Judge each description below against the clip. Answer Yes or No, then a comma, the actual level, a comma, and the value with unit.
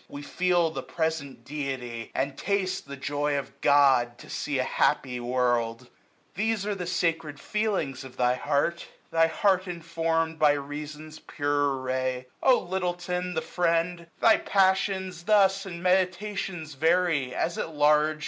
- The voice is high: No, medium, 160 Hz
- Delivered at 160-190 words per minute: No, average, 150 wpm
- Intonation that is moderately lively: Yes, average, 4.3 semitones